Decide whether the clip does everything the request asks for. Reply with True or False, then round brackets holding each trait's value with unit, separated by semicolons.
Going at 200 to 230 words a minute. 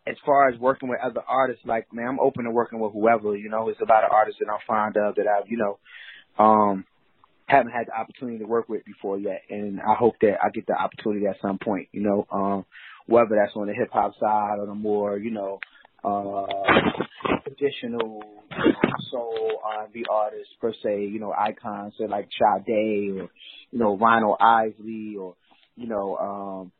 True (205 wpm)